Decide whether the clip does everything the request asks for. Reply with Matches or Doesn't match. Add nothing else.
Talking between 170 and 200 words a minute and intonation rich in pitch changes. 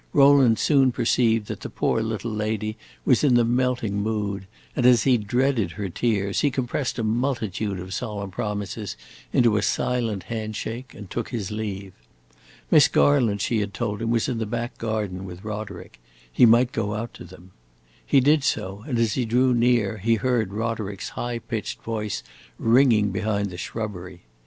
Doesn't match